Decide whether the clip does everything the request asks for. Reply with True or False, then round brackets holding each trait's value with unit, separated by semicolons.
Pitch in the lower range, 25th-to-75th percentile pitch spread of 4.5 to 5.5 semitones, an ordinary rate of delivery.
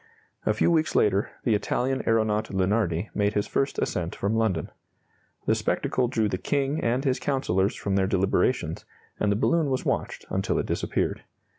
True (110 Hz; 4.9 semitones; 170 wpm)